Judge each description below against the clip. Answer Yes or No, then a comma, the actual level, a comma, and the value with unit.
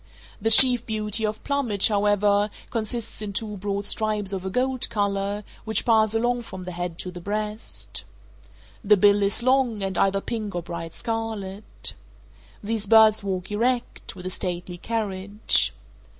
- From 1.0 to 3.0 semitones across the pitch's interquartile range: Yes, narrow, 2.5 semitones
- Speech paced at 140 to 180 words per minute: Yes, average, 155 wpm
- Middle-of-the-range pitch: No, high, 210 Hz